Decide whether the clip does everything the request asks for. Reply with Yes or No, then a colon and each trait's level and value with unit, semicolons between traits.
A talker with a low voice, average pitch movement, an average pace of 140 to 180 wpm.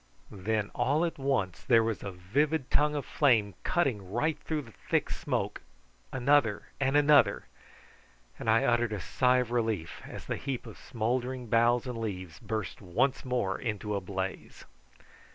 Yes: low, 115 Hz; average, 4.6 semitones; average, 160 wpm